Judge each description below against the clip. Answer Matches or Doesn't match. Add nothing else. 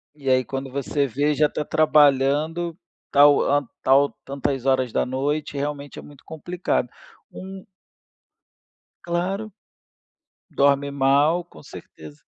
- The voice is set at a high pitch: Doesn't match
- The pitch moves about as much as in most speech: Doesn't match